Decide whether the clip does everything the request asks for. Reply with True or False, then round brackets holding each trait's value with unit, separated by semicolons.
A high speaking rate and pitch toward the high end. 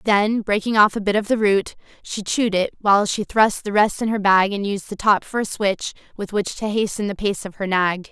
True (260 wpm; 205 Hz)